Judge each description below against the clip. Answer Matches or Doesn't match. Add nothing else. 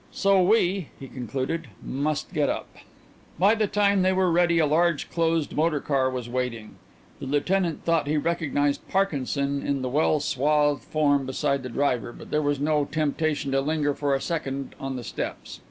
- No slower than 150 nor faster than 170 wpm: Doesn't match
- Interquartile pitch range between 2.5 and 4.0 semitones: Matches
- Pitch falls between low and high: Matches